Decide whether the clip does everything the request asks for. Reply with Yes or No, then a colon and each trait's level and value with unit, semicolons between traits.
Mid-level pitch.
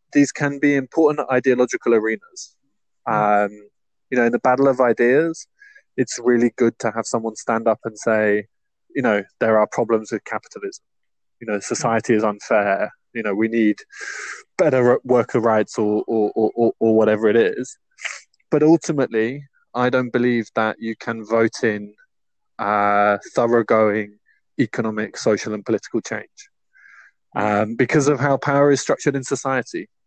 No: low, 115 Hz